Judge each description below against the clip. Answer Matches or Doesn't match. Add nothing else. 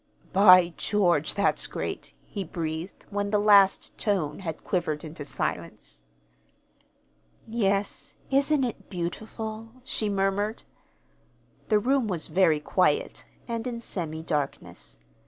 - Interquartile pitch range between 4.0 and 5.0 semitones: Matches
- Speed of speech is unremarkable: Doesn't match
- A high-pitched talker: Matches